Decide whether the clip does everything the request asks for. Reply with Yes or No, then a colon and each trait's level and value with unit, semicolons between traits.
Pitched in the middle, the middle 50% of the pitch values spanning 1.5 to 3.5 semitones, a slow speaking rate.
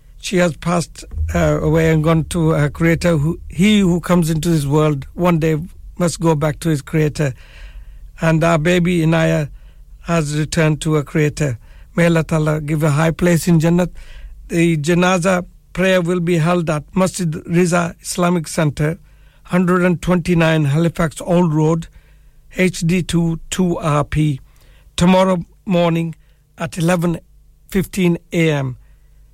Yes: medium, 165 Hz; narrow, 2.4 semitones; slow, 130 wpm